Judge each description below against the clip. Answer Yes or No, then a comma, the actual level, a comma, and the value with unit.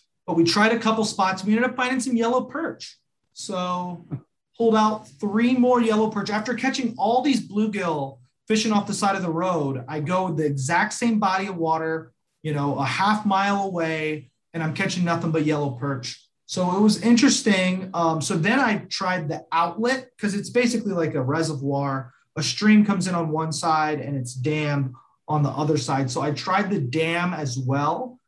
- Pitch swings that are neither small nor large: No, wide, 5.7 semitones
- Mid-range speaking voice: Yes, medium, 180 Hz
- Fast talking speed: No, average, 195 wpm